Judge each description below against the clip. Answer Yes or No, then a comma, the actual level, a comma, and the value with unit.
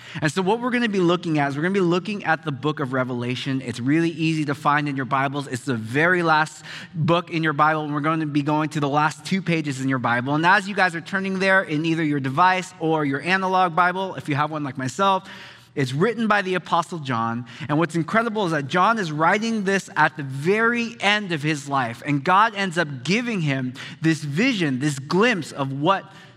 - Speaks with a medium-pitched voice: Yes, medium, 160 Hz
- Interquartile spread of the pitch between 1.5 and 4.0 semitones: No, average, 4.5 semitones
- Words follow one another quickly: Yes, fast, 240 wpm